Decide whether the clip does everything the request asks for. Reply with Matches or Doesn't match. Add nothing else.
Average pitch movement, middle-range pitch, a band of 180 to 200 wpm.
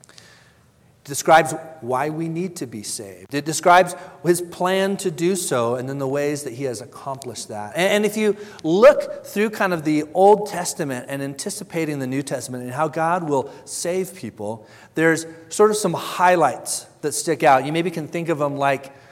Matches